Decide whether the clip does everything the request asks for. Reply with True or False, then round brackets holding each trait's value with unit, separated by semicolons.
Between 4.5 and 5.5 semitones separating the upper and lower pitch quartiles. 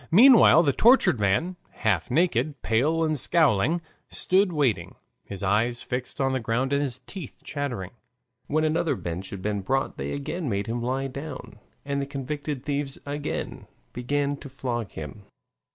True (4.9 semitones)